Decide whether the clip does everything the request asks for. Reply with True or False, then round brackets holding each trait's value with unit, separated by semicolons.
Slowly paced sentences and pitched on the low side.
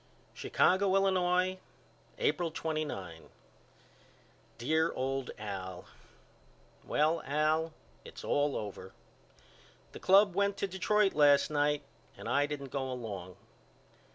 False (100 wpm; 150 Hz)